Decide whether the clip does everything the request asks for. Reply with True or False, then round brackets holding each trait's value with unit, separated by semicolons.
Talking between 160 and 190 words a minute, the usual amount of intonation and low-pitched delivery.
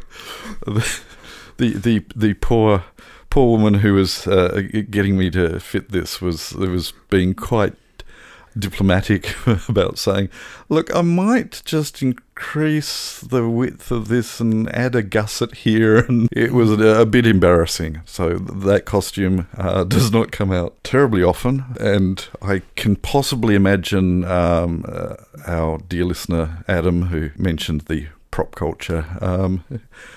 False (135 wpm; 4.5 semitones; 100 Hz)